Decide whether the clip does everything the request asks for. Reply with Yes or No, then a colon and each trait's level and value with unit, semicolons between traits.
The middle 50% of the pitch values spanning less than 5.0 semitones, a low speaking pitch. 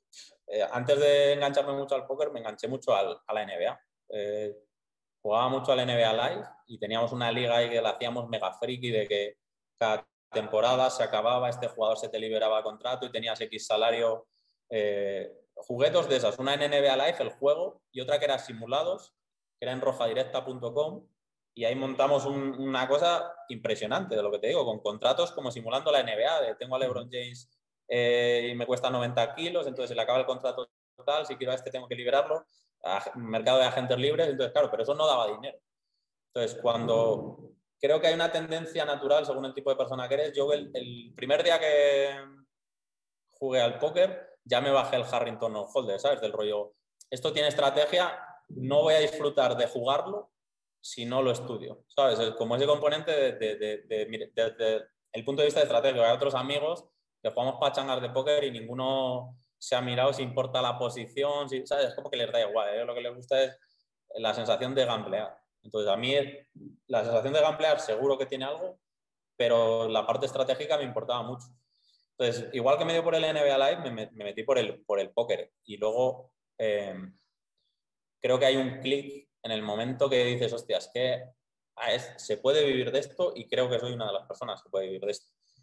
Yes: average, 3.7 semitones; low, 130 Hz